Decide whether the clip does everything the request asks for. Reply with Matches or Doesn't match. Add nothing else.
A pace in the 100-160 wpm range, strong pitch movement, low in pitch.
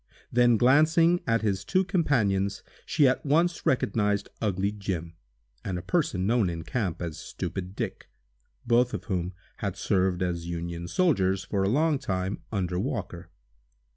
Matches